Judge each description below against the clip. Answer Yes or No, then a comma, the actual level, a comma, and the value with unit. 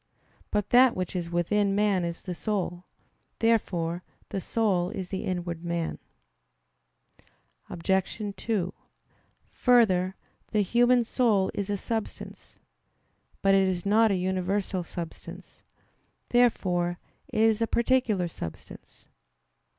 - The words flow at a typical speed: No, slow, 115 wpm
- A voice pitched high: Yes, high, 195 Hz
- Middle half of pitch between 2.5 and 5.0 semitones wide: Yes, average, 3.7 semitones